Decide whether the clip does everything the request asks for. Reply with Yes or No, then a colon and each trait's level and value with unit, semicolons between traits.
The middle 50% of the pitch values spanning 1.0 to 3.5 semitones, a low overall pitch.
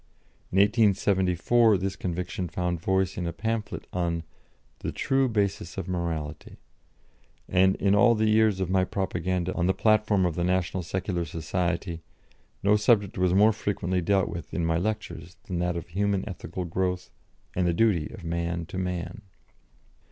Yes: average, 2.7 semitones; very low, 90 Hz